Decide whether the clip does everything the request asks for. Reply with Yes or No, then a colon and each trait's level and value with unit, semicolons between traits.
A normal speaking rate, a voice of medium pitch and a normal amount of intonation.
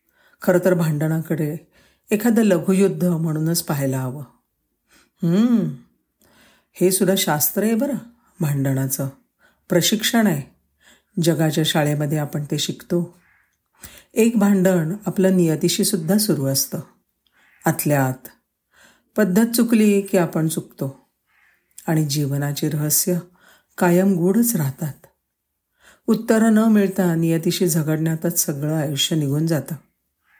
Yes: average, 105 wpm; medium, 175 Hz; average, 4.2 semitones